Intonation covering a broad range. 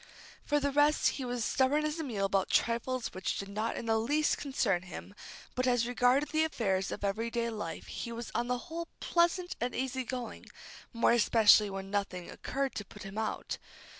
No: average, 4.9 semitones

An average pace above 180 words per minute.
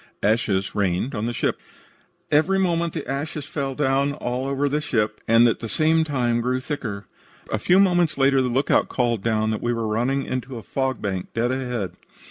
Yes: average, 195 wpm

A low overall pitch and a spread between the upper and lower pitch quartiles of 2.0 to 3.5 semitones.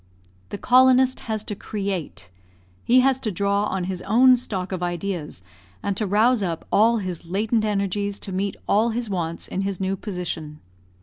No: high, 200 Hz; average, 3.2 semitones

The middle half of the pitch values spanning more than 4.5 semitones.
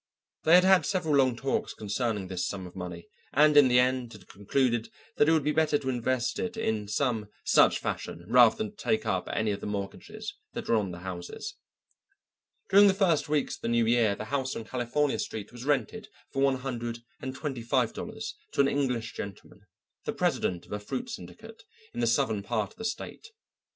Yes: wide, 5.5 semitones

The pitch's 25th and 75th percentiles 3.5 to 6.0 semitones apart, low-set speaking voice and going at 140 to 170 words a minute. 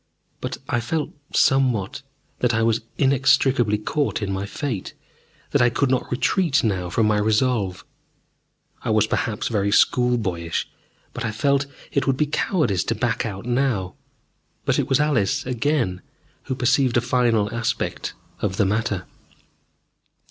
Yes: average, 4.2 semitones; low, 120 Hz; average, 155 wpm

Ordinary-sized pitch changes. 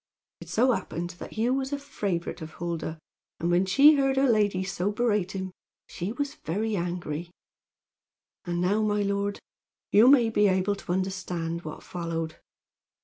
Yes: average, 4.2 semitones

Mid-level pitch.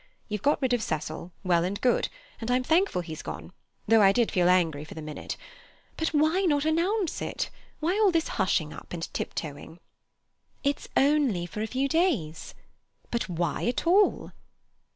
No: high, 225 Hz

